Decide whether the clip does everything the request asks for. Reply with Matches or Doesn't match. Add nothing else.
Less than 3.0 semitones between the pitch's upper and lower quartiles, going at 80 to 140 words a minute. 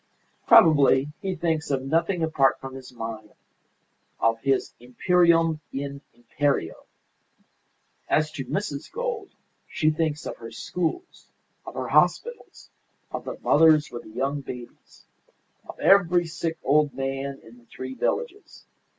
Doesn't match